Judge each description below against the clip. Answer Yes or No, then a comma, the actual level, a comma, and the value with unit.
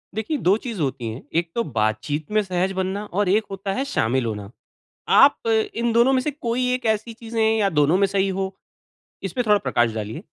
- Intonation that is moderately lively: No, wide, 7.8 semitones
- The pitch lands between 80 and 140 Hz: No, high, 195 Hz